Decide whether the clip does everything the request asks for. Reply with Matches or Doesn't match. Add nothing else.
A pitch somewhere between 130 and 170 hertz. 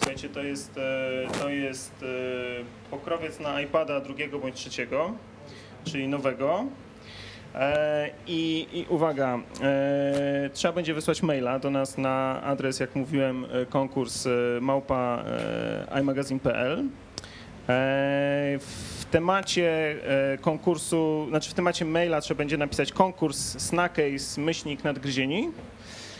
Matches